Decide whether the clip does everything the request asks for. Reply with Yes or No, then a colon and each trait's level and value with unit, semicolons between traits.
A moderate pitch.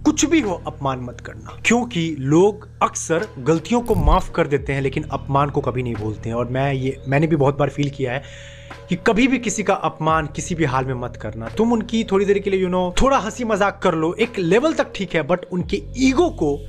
Yes: medium, 160 Hz